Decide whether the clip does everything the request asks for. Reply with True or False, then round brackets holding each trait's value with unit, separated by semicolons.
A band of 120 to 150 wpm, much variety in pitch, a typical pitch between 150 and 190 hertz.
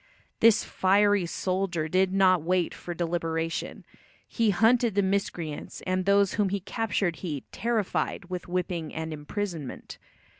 False (135 wpm; 3.0 semitones; 185 Hz)